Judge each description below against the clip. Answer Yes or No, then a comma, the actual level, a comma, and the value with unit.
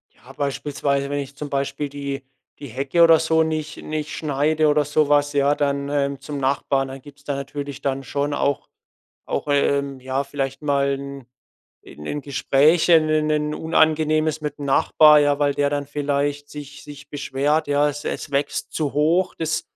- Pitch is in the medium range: Yes, medium, 145 Hz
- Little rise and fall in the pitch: Yes, narrow, 1.3 semitones